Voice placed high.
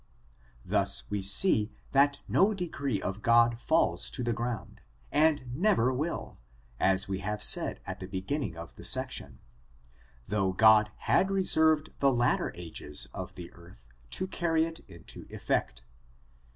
No: low, 120 Hz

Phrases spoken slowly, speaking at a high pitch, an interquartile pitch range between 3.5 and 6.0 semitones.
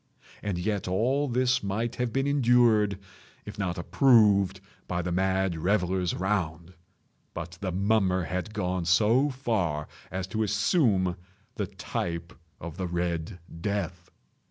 No: slow, 130 wpm; very low, 95 Hz; average, 3.8 semitones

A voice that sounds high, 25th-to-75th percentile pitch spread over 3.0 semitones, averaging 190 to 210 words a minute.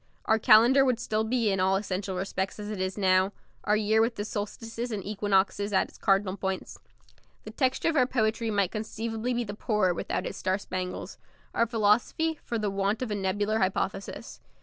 No: high, 210 Hz; average, 2.7 semitones; average, 195 wpm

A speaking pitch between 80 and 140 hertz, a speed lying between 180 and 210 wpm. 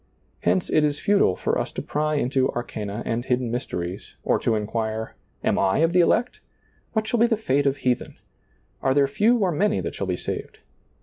Yes: low, 135 Hz; average, 200 wpm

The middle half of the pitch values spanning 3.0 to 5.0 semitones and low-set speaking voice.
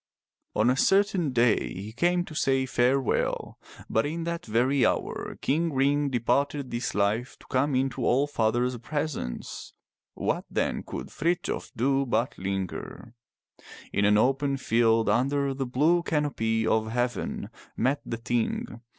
Yes: average, 3.8 semitones; low, 130 Hz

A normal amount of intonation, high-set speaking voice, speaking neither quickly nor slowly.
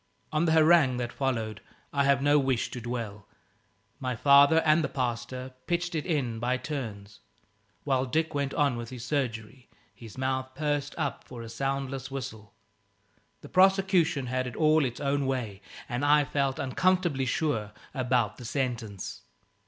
No: average, 3.3 semitones; low, 135 Hz; average, 160 wpm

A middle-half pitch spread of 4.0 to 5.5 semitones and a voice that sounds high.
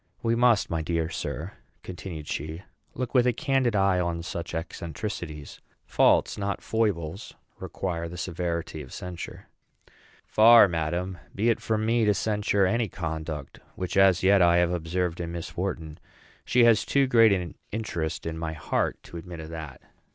No: average, 4.3 semitones; very low, 90 Hz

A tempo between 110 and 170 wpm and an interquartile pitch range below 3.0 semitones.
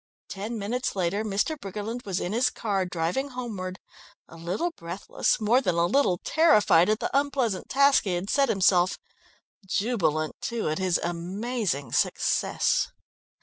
No: average, 145 wpm; wide, 5.4 semitones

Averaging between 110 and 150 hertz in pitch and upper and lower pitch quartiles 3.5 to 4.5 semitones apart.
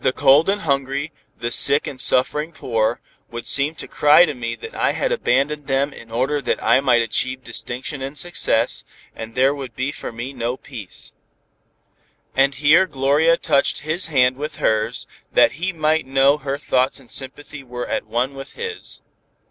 No: low, 135 Hz; average, 2.9 semitones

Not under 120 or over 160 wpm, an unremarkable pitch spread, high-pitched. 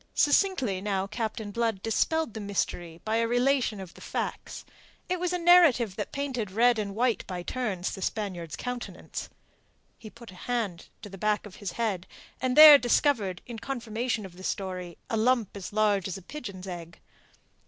No: average, 180 wpm; average, 4.3 semitones; high, 215 Hz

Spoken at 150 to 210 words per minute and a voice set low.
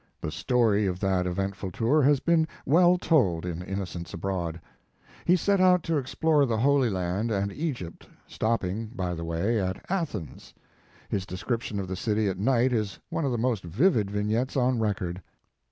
Yes: average, 170 wpm; low, 105 Hz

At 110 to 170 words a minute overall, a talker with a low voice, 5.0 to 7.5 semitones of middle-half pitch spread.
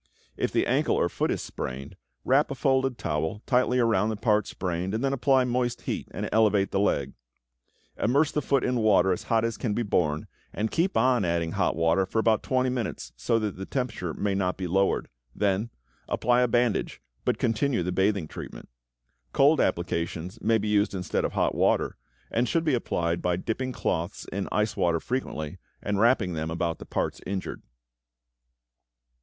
No: average, 185 wpm; low, 105 Hz; wide, 5.5 semitones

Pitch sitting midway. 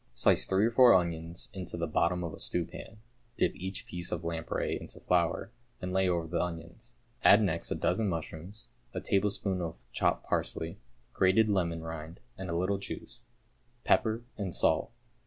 No: very low, 90 Hz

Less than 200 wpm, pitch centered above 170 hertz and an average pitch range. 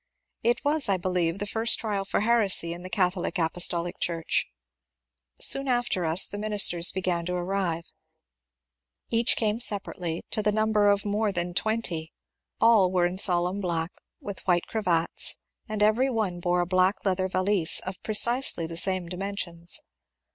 Yes: average, 160 wpm; high, 190 Hz; average, 3.4 semitones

